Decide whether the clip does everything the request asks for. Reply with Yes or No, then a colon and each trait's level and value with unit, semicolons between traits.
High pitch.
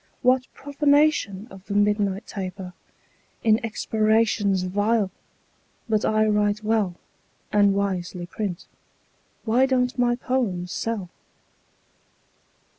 Yes: high, 210 Hz